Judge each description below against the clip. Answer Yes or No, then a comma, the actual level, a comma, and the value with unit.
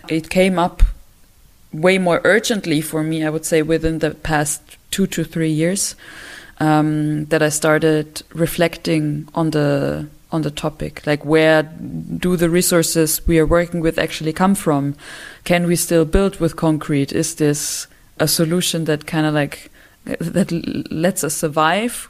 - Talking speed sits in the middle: Yes, average, 160 wpm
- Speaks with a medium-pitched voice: Yes, medium, 160 Hz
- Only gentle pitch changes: Yes, narrow, 1.8 semitones